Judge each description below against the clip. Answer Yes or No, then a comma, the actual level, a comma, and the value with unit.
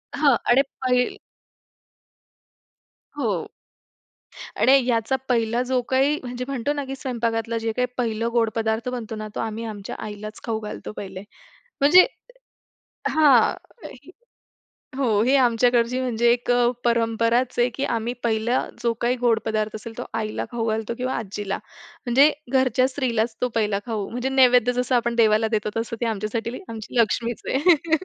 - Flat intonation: Yes, narrow, 2.2 semitones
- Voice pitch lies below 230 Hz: No, high, 235 Hz